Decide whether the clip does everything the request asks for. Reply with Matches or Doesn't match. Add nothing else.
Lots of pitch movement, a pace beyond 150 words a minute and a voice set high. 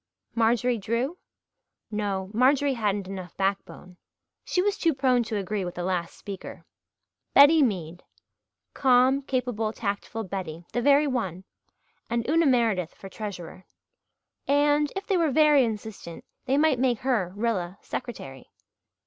Doesn't match